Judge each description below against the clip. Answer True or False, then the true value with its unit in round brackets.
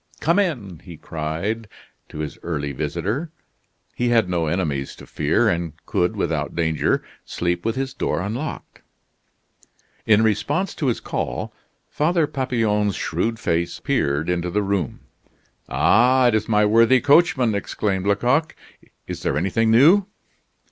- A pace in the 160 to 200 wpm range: False (140 wpm)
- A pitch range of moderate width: False (6.8 semitones)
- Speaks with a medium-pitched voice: False (105 Hz)